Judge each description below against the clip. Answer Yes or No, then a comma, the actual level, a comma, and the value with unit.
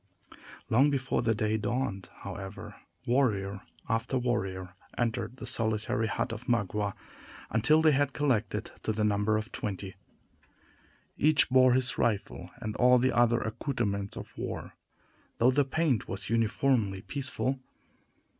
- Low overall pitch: Yes, low, 115 Hz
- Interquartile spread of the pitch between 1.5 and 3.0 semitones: No, average, 3.8 semitones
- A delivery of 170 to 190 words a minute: No, slow, 135 wpm